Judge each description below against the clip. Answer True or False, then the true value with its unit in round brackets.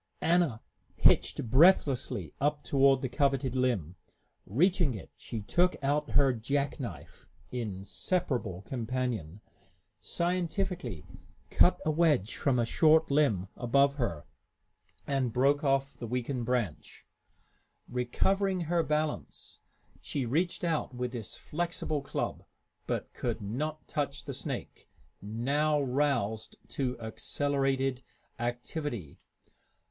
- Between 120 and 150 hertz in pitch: True (135 Hz)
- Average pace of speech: False (110 wpm)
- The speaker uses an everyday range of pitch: True (4.2 semitones)